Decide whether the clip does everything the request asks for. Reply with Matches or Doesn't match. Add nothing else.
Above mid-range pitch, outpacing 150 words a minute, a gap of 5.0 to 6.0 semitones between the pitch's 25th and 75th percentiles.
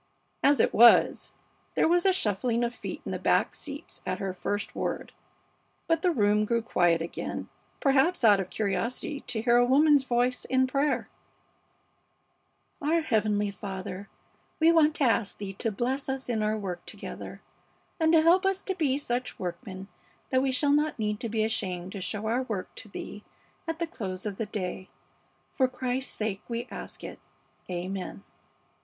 Matches